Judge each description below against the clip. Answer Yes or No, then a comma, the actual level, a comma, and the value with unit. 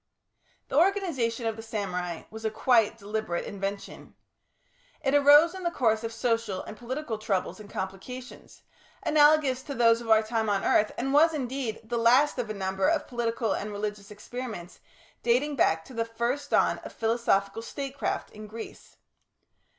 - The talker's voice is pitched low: No, high, 230 Hz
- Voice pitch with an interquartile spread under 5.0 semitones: Yes, average, 3.9 semitones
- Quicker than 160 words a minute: Yes, average, 170 wpm